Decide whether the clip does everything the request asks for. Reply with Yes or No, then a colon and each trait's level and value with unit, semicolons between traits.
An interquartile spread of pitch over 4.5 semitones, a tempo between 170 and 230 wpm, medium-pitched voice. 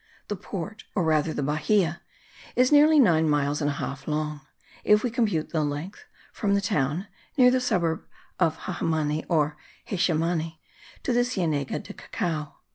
No: average, 5.3 semitones; average, 160 wpm; medium, 165 Hz